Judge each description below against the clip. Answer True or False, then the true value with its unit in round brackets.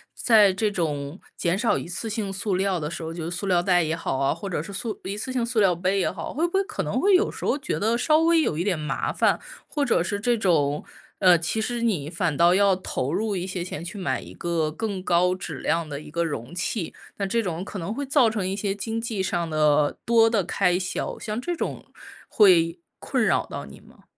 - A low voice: False (190 Hz)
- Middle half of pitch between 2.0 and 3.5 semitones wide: False (4.6 semitones)